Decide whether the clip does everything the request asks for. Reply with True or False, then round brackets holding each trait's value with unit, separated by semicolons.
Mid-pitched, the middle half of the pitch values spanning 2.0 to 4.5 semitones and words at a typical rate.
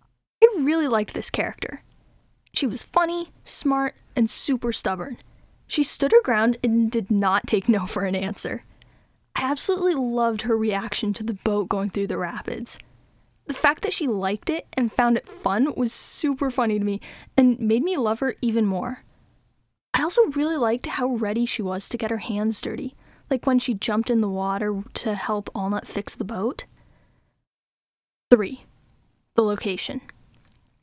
False (230 Hz; 4.2 semitones; 170 wpm)